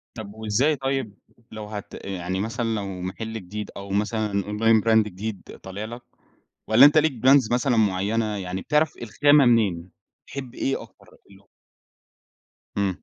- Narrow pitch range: No, average, 3.4 semitones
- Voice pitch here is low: Yes, low, 110 Hz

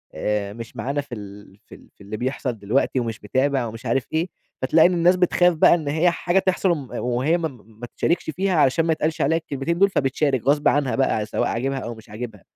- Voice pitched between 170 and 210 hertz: No, low, 135 Hz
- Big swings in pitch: Yes, wide, 6.0 semitones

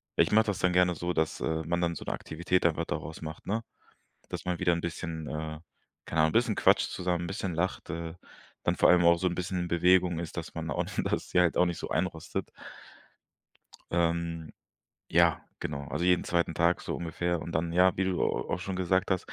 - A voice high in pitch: No, very low, 85 Hz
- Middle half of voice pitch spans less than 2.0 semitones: Yes, narrow, 1.6 semitones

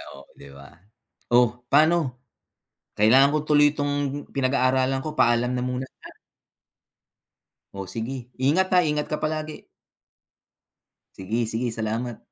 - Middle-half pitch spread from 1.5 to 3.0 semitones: No, average, 3.8 semitones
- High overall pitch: No, low, 130 Hz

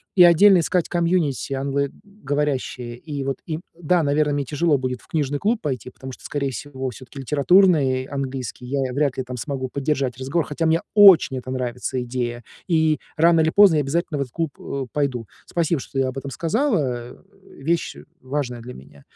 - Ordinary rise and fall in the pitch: Yes, average, 3.9 semitones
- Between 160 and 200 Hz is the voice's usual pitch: No, medium, 140 Hz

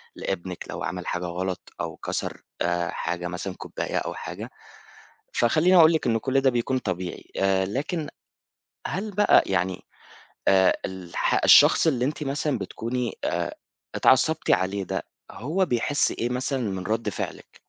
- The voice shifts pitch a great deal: Yes, wide, 7.0 semitones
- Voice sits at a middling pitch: No, low, 115 Hz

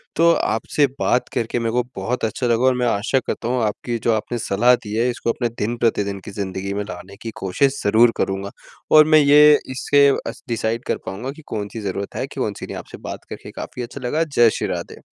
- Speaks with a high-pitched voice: No, low, 115 Hz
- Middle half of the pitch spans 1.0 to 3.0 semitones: No, average, 3.6 semitones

